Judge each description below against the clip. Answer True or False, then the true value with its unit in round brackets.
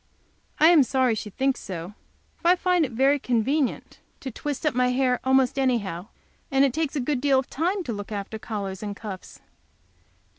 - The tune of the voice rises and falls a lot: False (4.6 semitones)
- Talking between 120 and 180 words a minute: False (195 wpm)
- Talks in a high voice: True (260 Hz)